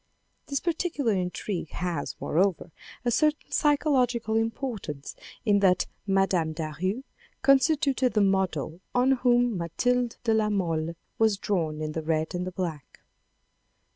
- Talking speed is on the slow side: Yes, slow, 130 wpm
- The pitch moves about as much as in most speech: No, wide, 6.7 semitones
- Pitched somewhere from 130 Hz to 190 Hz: No, high, 200 Hz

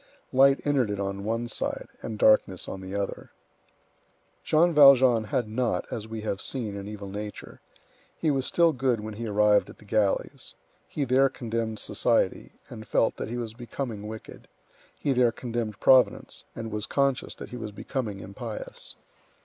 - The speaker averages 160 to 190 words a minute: Yes, average, 170 wpm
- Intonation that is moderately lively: Yes, average, 3.5 semitones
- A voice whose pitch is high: No, low, 115 Hz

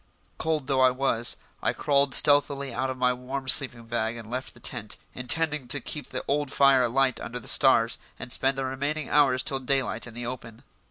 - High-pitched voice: No, low, 130 Hz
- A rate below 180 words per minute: No, fast, 205 wpm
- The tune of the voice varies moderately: No, narrow, 2.1 semitones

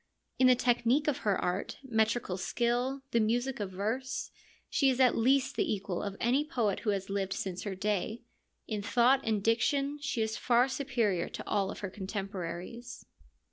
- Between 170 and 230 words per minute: Yes, average, 175 wpm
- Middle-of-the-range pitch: No, high, 230 Hz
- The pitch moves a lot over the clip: No, average, 4.3 semitones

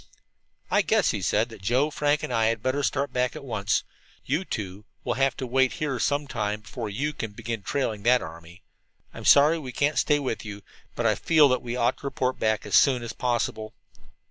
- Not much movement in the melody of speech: No, average, 4.3 semitones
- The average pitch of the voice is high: No, low, 125 Hz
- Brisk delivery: Yes, fast, 215 wpm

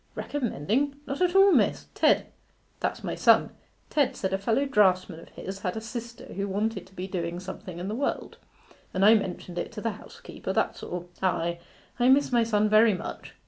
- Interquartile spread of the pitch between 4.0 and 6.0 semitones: Yes, average, 4.6 semitones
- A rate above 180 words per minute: Yes, average, 195 wpm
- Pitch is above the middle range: Yes, high, 210 Hz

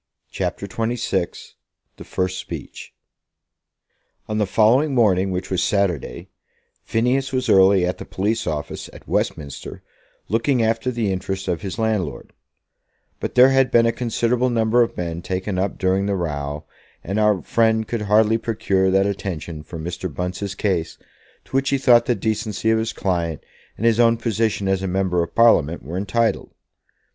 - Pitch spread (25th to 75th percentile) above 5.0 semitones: No, average, 3.8 semitones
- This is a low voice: Yes, low, 100 Hz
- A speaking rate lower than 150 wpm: No, average, 165 wpm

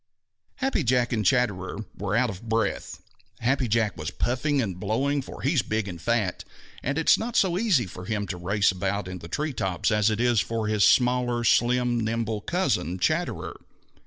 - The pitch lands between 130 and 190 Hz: No, low, 115 Hz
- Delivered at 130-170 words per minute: No, average, 195 wpm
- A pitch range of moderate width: Yes, average, 3.8 semitones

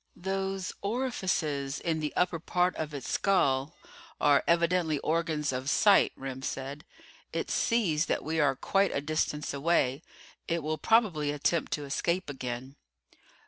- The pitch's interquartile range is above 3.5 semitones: Yes, average, 4.2 semitones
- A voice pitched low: No, medium, 155 Hz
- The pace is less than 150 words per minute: Yes, average, 140 wpm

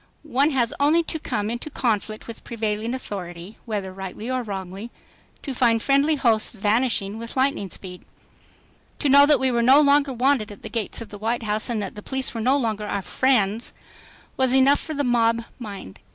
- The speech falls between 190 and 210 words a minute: Yes, average, 195 wpm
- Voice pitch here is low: No, high, 230 Hz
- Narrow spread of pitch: No, average, 4.1 semitones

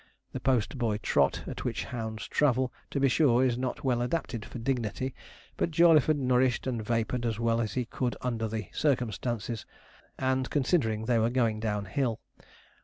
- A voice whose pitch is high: No, low, 120 Hz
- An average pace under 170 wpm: No, average, 175 wpm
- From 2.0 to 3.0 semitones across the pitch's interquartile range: Yes, average, 2.7 semitones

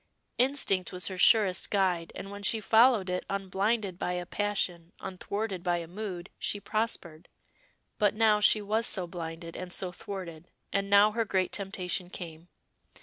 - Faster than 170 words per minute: No, average, 160 wpm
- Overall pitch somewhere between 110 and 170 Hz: No, high, 190 Hz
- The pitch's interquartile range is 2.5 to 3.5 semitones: Yes, average, 2.8 semitones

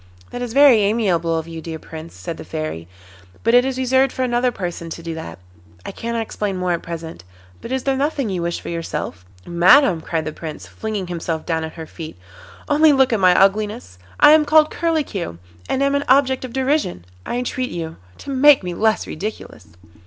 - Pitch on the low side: No, high, 205 Hz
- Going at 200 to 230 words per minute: Yes, fast, 205 wpm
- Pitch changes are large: Yes, wide, 7.9 semitones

